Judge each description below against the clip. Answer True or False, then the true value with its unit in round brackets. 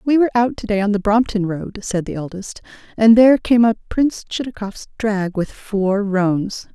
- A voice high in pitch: True (210 Hz)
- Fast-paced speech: False (195 wpm)